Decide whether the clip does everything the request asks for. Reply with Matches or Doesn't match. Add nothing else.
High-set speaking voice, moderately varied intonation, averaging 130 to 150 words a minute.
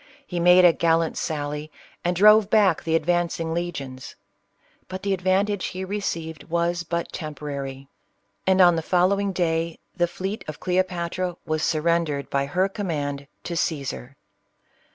Doesn't match